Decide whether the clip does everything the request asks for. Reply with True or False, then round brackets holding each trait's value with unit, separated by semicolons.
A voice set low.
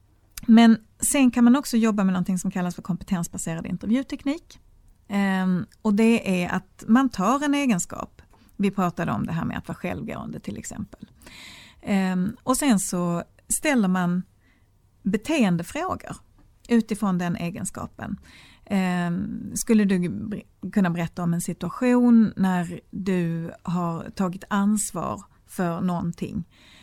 False (190 Hz)